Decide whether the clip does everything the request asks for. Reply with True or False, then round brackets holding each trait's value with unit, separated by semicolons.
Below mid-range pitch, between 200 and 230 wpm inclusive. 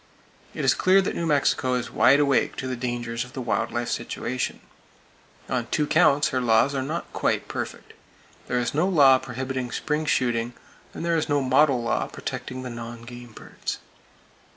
False (130 Hz; 190 wpm)